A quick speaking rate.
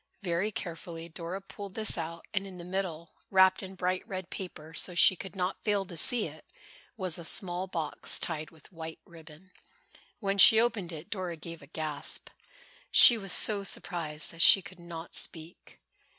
No: average, 180 wpm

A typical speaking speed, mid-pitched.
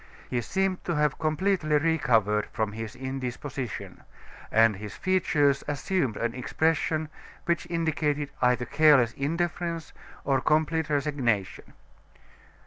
No: slow, 110 wpm; medium, 145 Hz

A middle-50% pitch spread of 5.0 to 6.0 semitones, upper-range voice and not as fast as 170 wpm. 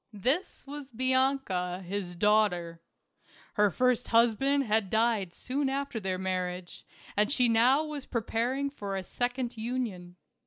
Yes: wide, 5.5 semitones; high, 230 Hz; average, 140 wpm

